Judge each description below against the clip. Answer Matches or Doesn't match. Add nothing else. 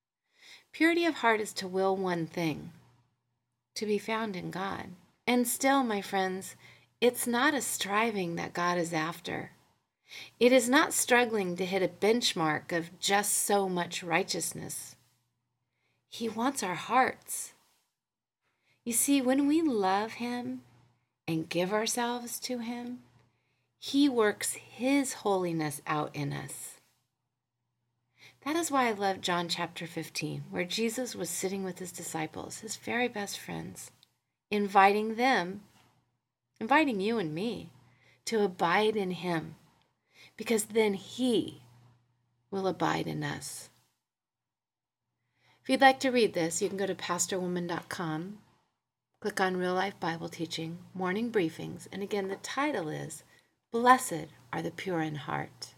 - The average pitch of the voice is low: Doesn't match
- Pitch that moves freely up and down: Matches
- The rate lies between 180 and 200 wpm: Doesn't match